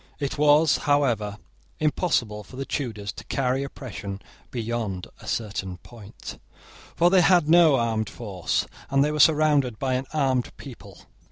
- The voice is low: Yes, low, 130 Hz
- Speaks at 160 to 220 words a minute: No, average, 150 wpm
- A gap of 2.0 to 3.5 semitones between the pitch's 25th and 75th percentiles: No, wide, 5.4 semitones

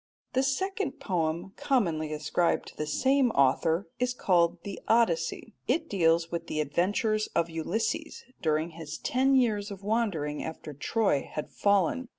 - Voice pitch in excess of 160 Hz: Yes, medium, 185 Hz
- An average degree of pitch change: No, wide, 6.7 semitones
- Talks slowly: No, average, 150 wpm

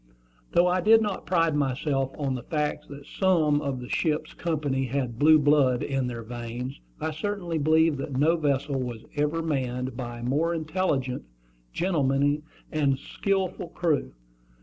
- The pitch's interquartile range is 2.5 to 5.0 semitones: Yes, average, 3.7 semitones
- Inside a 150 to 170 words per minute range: Yes, average, 155 wpm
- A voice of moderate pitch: Yes, medium, 145 Hz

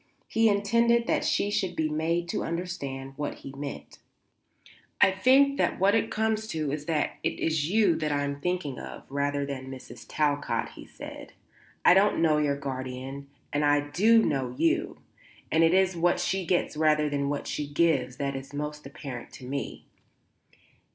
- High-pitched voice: No, medium, 150 Hz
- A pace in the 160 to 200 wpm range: Yes, average, 180 wpm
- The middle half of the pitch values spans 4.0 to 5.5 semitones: Yes, average, 4.6 semitones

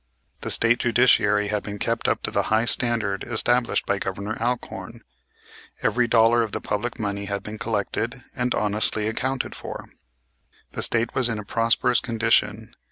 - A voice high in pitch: No, low, 115 Hz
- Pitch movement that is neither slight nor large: No, narrow, 2.3 semitones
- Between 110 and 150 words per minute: No, average, 165 wpm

